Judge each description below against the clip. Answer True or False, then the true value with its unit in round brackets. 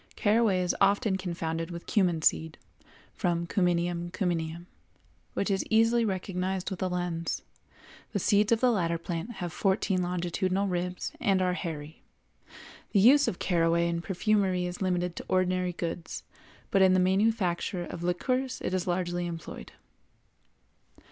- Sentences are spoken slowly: False (145 wpm)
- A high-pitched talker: False (180 Hz)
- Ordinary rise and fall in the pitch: False (2.2 semitones)